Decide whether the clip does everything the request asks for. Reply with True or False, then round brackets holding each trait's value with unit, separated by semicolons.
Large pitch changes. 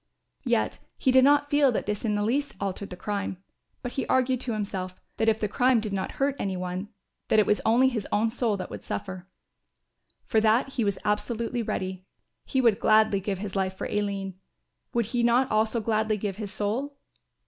False (3.5 semitones)